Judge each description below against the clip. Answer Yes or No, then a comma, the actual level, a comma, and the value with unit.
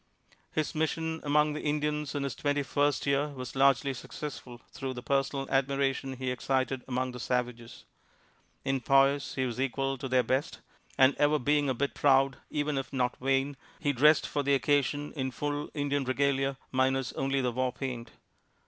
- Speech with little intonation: Yes, narrow, 1.8 semitones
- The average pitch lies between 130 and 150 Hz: Yes, low, 135 Hz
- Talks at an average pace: Yes, average, 175 wpm